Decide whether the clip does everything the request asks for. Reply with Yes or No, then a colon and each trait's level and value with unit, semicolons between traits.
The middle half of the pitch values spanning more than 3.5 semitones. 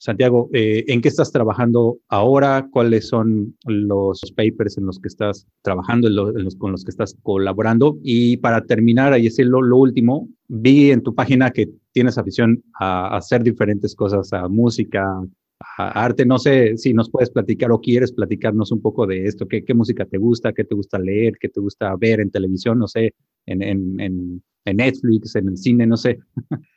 No: average, 3.2 semitones